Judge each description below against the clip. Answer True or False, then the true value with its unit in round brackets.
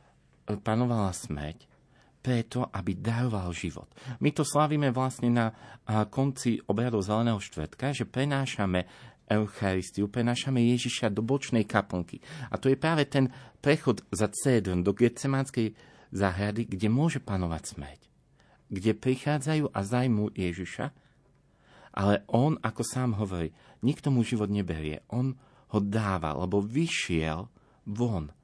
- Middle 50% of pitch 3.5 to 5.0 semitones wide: True (4.5 semitones)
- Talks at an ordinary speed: True (120 wpm)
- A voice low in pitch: True (115 Hz)